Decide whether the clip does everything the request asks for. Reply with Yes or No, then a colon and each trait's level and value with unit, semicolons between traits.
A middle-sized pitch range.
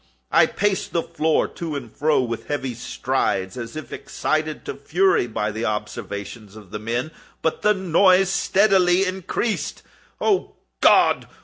No: wide, 8.4 semitones